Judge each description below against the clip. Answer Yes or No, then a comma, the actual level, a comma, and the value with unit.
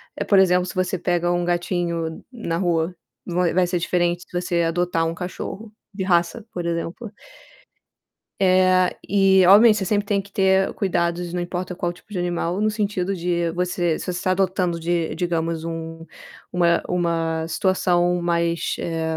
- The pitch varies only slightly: Yes, narrow, 1.7 semitones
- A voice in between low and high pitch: Yes, medium, 175 Hz